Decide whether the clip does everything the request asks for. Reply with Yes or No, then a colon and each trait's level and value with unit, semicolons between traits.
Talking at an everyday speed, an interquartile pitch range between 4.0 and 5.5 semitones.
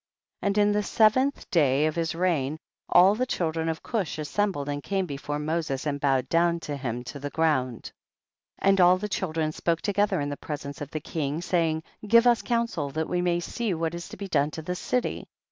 No: fast, 225 wpm; average, 4.9 semitones